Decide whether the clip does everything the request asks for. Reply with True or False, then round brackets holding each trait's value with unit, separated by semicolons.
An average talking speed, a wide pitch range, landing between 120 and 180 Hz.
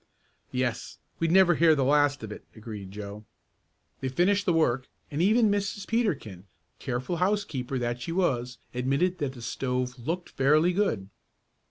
True (155 wpm; 6.6 semitones; 140 Hz)